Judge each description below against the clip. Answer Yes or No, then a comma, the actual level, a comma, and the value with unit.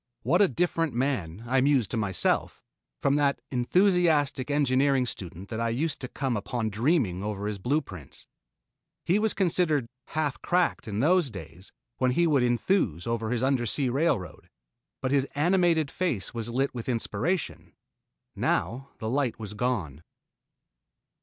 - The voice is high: No, low, 130 Hz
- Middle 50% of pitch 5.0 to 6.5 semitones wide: Yes, wide, 5.4 semitones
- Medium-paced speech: Yes, average, 150 wpm